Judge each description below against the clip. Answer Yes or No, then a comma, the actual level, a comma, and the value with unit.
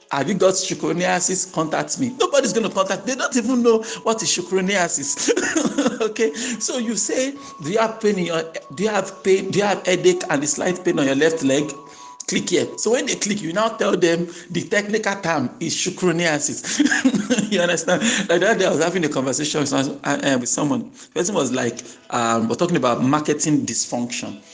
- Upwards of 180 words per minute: Yes, average, 195 wpm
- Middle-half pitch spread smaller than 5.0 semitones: No, wide, 5.5 semitones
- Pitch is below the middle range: No, medium, 185 Hz